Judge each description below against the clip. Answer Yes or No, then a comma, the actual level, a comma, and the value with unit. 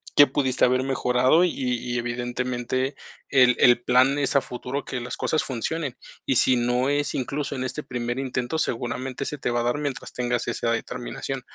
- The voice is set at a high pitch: No, low, 125 Hz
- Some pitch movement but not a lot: No, narrow, 1.9 semitones